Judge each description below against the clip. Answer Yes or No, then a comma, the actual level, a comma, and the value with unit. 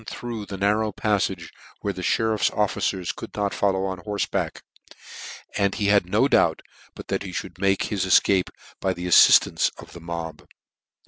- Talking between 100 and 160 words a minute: No, average, 170 wpm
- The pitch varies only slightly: Yes, narrow, 2.3 semitones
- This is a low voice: Yes, low, 100 Hz